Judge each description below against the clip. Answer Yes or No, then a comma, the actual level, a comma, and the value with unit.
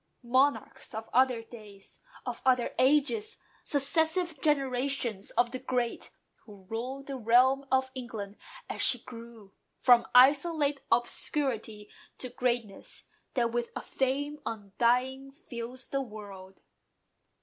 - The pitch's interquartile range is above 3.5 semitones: No, average, 3.1 semitones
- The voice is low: No, very high, 250 Hz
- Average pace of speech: No, slow, 115 wpm